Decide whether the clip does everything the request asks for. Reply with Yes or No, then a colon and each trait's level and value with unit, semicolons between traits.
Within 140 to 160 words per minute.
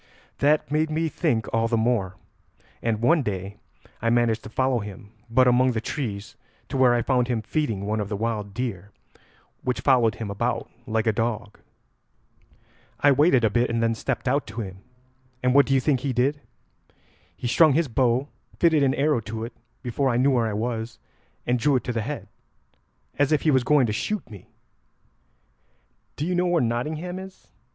No: average, 190 wpm